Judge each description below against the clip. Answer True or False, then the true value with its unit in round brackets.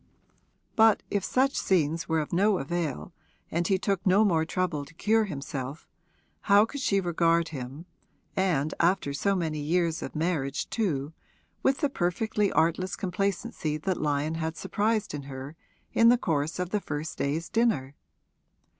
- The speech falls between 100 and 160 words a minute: True (155 wpm)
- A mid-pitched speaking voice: True (170 Hz)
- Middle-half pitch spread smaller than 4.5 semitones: False (4.8 semitones)